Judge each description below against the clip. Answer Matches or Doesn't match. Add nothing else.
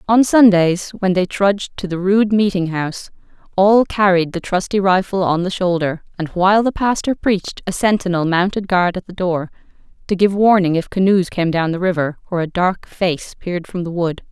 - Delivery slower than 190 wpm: Doesn't match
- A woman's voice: Matches